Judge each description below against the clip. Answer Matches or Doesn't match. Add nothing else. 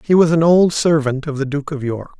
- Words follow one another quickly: Matches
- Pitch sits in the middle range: Matches